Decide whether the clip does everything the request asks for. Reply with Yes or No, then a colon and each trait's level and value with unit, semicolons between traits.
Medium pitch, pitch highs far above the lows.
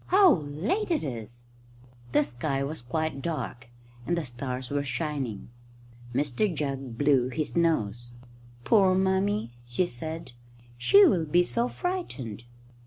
Yes: medium, 145 Hz; wide, 6.3 semitones